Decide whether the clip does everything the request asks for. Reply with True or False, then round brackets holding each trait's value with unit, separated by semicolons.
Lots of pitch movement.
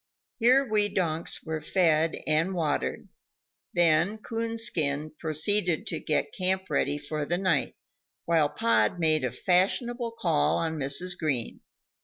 False (4.2 semitones)